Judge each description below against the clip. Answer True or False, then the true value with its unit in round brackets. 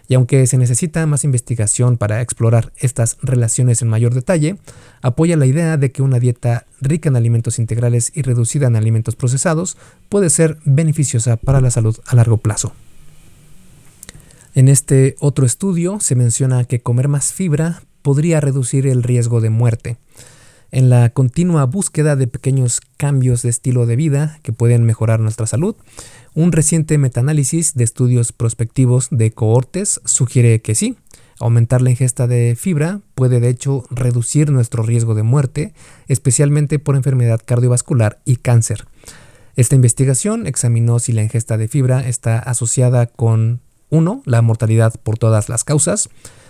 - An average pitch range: True (3.4 semitones)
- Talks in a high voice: False (125 Hz)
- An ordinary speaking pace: True (150 wpm)